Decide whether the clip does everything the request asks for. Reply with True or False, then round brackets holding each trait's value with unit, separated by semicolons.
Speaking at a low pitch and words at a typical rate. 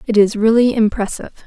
False (220 Hz; 165 wpm)